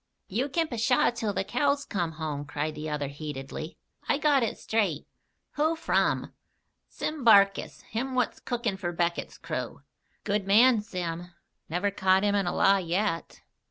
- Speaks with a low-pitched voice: No, high, 195 Hz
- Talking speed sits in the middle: Yes, average, 160 wpm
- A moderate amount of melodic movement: No, wide, 6.3 semitones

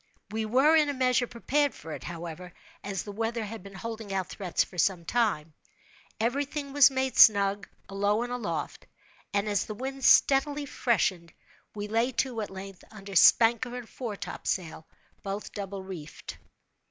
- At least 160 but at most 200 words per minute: Yes, average, 165 wpm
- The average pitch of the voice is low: No, high, 215 Hz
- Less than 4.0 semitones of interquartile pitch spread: No, average, 4.3 semitones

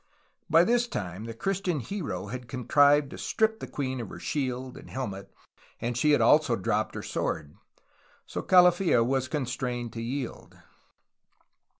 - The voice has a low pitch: Yes, low, 130 Hz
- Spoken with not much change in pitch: No, average, 4.8 semitones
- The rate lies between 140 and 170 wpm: Yes, average, 155 wpm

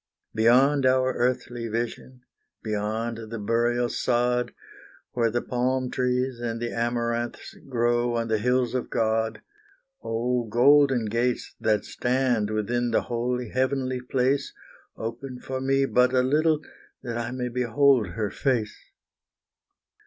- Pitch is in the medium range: No, low, 120 Hz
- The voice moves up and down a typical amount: No, narrow, 1.8 semitones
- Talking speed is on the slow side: Yes, slow, 130 wpm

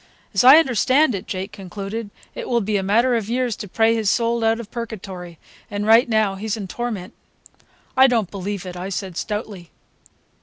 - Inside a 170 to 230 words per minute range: Yes, average, 190 wpm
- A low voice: No, high, 215 Hz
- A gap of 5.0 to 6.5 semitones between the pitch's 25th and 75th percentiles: No, average, 3.2 semitones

